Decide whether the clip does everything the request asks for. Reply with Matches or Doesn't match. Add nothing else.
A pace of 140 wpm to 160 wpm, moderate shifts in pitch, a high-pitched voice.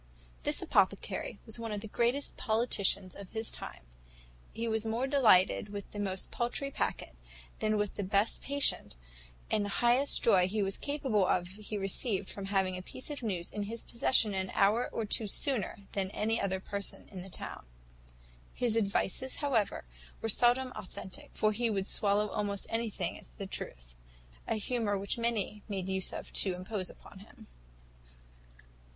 Doesn't match